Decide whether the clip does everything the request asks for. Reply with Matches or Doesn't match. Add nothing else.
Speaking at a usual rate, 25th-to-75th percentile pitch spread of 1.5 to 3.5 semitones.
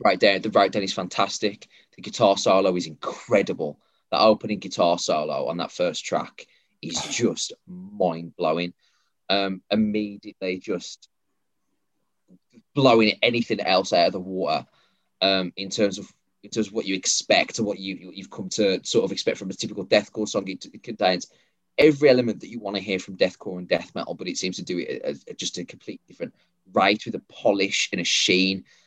Matches